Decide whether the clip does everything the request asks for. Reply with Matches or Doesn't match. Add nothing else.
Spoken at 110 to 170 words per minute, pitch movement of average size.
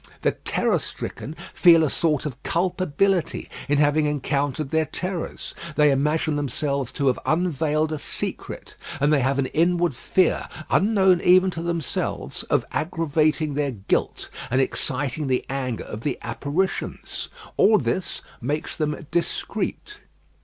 Matches